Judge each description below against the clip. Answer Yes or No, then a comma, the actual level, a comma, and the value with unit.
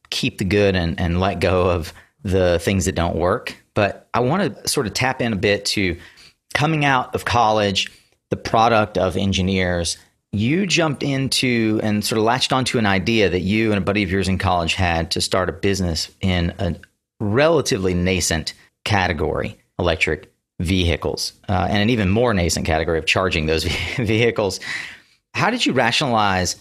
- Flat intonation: No, average, 3.8 semitones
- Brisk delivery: No, average, 175 wpm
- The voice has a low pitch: Yes, very low, 95 Hz